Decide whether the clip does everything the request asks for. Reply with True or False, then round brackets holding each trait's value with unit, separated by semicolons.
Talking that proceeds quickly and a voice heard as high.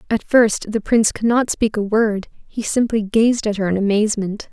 True (210 wpm; 215 Hz)